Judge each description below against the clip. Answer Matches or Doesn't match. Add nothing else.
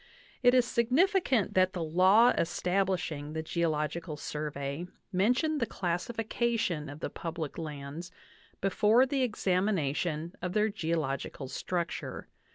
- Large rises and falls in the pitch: Matches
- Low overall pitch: Doesn't match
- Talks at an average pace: Doesn't match